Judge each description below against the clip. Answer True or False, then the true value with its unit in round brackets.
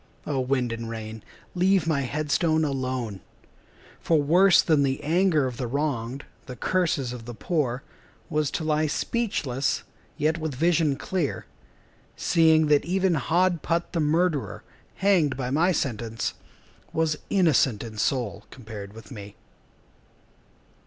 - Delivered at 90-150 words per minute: True (140 wpm)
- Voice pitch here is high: False (145 Hz)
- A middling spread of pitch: True (4.9 semitones)